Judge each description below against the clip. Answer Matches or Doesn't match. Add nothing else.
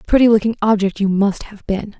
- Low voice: Doesn't match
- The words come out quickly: Matches